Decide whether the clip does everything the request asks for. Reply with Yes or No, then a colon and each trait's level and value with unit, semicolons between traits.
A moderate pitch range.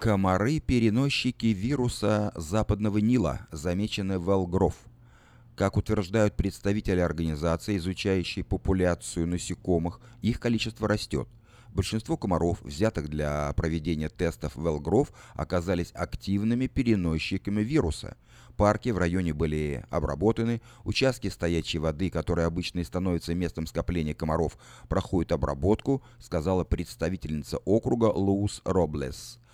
Yes: average, 4.6 semitones